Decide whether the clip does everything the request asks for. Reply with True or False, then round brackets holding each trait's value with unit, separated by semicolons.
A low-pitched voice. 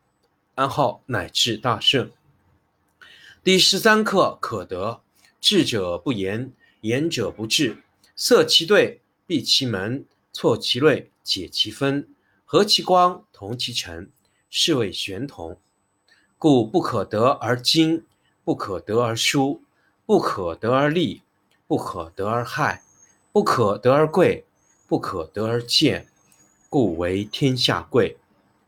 True (120 Hz)